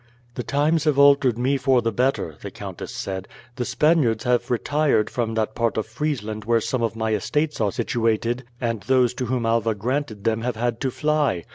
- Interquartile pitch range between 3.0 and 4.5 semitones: Yes, average, 3.4 semitones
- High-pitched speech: No, low, 120 Hz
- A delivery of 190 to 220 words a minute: Yes, average, 195 wpm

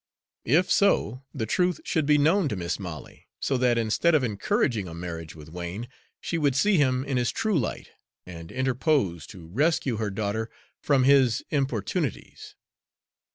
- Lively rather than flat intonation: Yes, wide, 6.8 semitones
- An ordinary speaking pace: Yes, average, 160 wpm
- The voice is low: Yes, low, 125 Hz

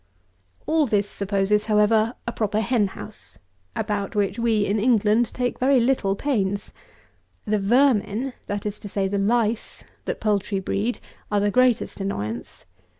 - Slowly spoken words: No, average, 150 wpm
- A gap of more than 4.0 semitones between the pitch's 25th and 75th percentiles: No, average, 2.8 semitones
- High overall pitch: Yes, high, 210 Hz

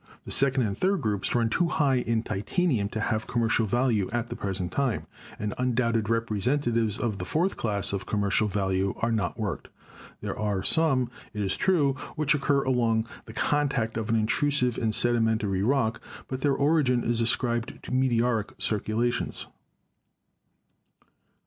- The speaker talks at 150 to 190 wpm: Yes, average, 160 wpm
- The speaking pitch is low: Yes, low, 115 Hz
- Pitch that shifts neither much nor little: Yes, average, 3.6 semitones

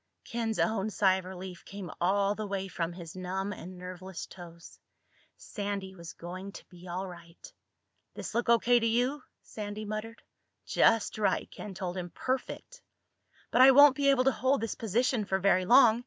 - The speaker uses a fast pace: No, average, 175 wpm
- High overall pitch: Yes, high, 200 Hz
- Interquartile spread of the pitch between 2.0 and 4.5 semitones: Yes, average, 3.8 semitones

